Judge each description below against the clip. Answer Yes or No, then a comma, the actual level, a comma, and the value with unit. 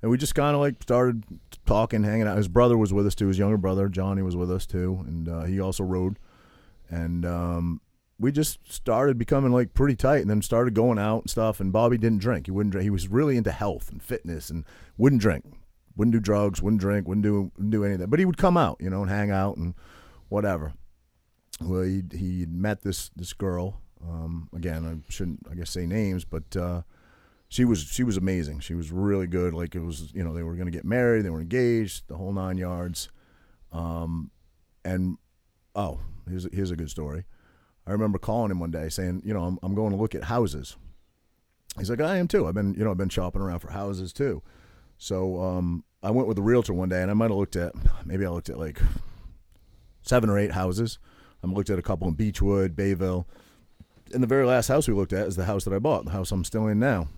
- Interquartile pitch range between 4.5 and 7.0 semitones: No, average, 3.8 semitones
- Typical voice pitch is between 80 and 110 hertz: Yes, very low, 95 Hz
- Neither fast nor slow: No, fast, 230 wpm